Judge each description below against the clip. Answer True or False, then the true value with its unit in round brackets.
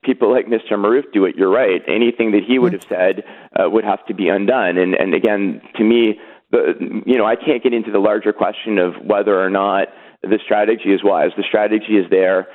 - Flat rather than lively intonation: False (3.4 semitones)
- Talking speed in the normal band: False (225 wpm)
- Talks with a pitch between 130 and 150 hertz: False (110 Hz)